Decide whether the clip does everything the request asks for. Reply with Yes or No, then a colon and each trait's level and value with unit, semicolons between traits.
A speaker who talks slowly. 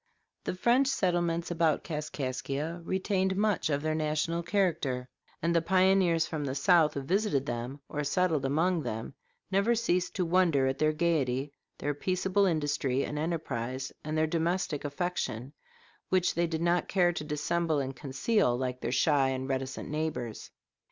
No: average, 160 wpm